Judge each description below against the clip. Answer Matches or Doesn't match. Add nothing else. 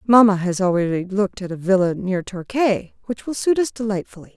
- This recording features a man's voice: Doesn't match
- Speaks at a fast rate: Doesn't match